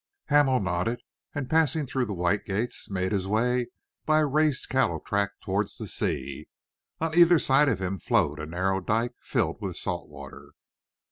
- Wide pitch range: Yes, wide, 6.7 semitones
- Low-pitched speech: Yes, low, 110 Hz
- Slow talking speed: No, average, 175 wpm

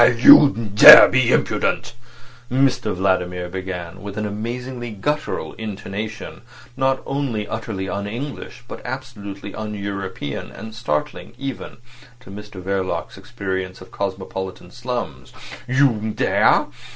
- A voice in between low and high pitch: No, low, 105 Hz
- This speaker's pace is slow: Yes, slow, 120 wpm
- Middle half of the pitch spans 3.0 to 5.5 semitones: Yes, average, 4.1 semitones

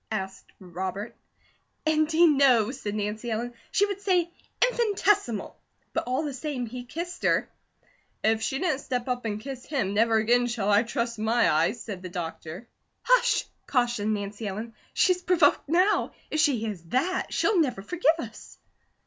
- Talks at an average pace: Yes, average, 160 wpm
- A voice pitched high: Yes, high, 245 Hz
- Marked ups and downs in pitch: Yes, wide, 6.6 semitones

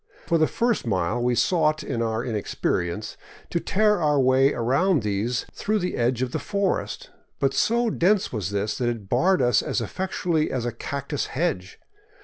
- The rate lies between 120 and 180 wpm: Yes, average, 175 wpm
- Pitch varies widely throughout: Yes, wide, 7.2 semitones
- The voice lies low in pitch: Yes, low, 130 Hz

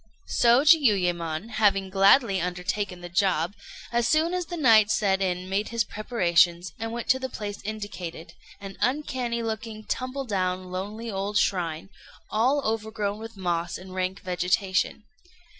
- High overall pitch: Yes, high, 205 Hz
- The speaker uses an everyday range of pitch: Yes, average, 3.9 semitones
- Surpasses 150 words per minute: No, average, 145 wpm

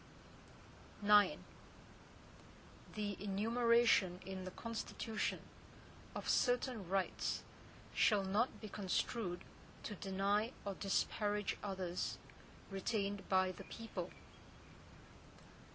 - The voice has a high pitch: Yes, high, 205 Hz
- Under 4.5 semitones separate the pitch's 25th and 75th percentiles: Yes, narrow, 2.6 semitones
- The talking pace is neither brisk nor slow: No, slow, 85 wpm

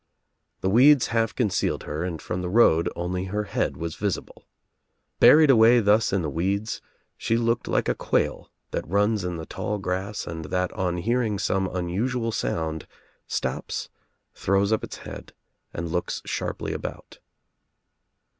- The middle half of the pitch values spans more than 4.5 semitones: No, average, 4.2 semitones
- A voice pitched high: No, low, 100 Hz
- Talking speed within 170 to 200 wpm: No, average, 155 wpm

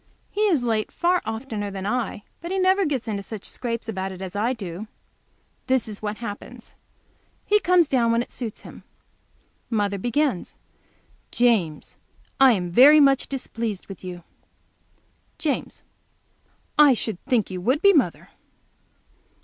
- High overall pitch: Yes, high, 230 Hz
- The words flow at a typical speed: Yes, average, 150 wpm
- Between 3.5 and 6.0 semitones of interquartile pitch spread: Yes, average, 5.2 semitones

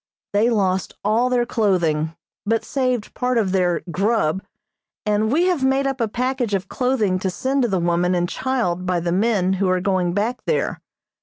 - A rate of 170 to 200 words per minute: Yes, average, 185 wpm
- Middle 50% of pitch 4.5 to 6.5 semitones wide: Yes, average, 5.3 semitones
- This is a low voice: No, high, 205 Hz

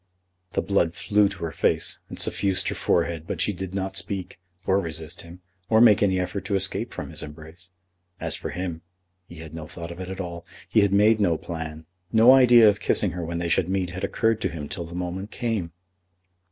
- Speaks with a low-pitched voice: Yes, very low, 90 Hz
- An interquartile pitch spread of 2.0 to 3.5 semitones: Yes, average, 3.1 semitones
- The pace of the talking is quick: Yes, fast, 220 wpm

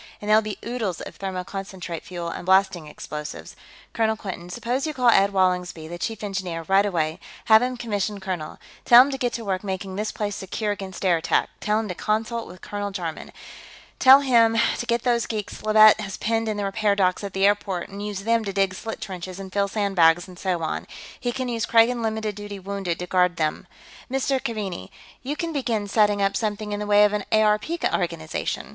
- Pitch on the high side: Yes, high, 205 Hz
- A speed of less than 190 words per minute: No, fast, 205 wpm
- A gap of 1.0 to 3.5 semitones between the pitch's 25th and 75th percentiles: Yes, average, 3.0 semitones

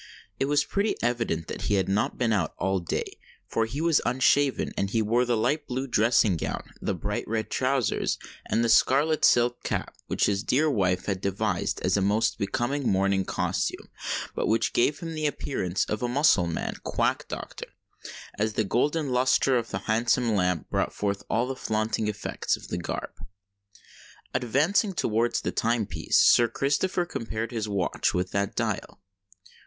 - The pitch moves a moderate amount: Yes, average, 4.8 semitones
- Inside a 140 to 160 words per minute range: No, average, 170 wpm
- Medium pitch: No, low, 115 Hz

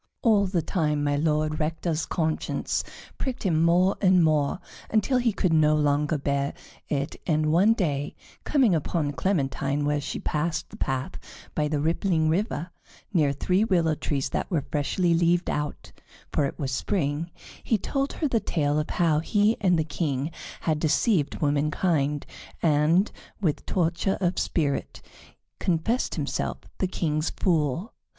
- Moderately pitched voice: Yes, medium, 160 Hz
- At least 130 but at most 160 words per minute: Yes, average, 150 wpm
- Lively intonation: No, average, 3.7 semitones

